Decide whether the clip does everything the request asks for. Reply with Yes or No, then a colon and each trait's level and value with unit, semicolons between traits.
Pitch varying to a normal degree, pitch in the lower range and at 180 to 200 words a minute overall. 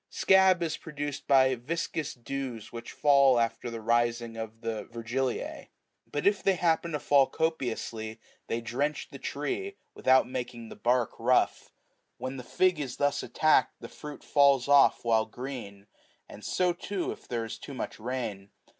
No: average, 4.1 semitones; low, 130 Hz; average, 165 wpm